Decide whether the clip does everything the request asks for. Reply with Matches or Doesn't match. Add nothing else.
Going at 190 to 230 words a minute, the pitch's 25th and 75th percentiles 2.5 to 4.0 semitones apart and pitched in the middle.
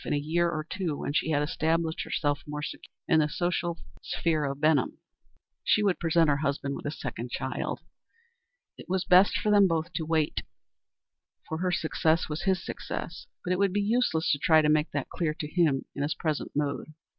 Matches